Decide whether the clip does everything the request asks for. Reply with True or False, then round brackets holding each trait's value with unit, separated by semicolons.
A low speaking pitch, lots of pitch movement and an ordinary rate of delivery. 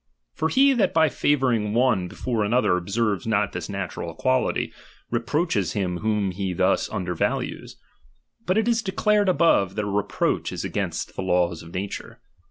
True (105 Hz; 7.8 semitones; 170 wpm)